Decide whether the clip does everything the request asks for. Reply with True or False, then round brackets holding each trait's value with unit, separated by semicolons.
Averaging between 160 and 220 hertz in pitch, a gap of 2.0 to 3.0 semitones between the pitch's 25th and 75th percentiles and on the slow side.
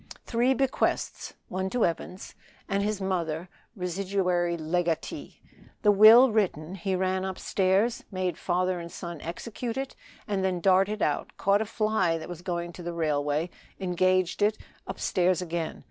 False (185 Hz; 2.7 semitones; 145 wpm)